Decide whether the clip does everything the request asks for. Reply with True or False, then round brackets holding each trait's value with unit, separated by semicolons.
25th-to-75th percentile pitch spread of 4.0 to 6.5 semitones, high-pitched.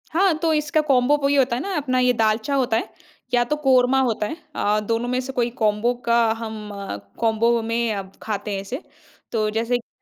False (3.4 semitones; 240 Hz)